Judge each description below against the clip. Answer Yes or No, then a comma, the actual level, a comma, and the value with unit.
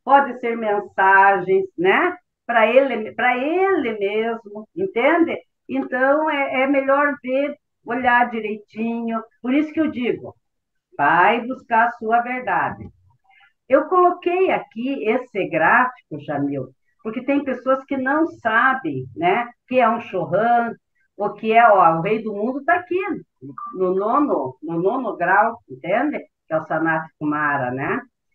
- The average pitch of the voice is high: Yes, high, 240 Hz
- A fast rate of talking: No, average, 140 wpm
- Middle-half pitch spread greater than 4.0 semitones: Yes, average, 5.2 semitones